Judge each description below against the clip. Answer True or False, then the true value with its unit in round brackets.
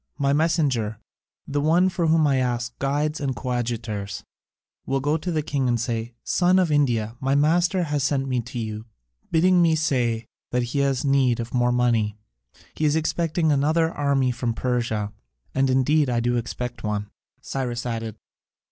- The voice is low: True (130 Hz)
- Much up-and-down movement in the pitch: False (4.2 semitones)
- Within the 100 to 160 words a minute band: False (170 wpm)